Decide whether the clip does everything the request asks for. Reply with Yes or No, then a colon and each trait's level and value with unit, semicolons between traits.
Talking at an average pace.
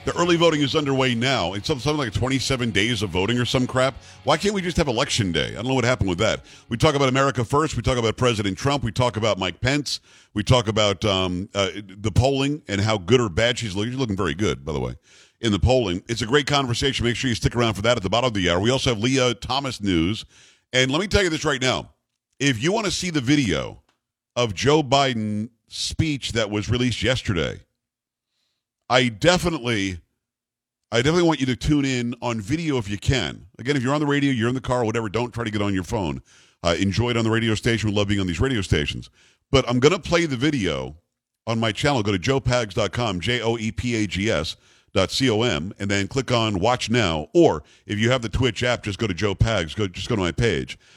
No: fast, 235 wpm